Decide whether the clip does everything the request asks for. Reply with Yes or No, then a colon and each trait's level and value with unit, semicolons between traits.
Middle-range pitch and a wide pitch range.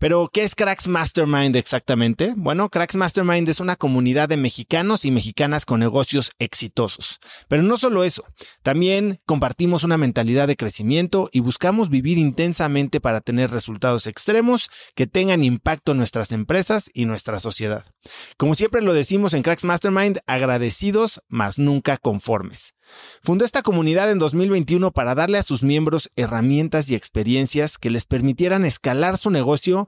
Yes: medium, 150 Hz; wide, 6.5 semitones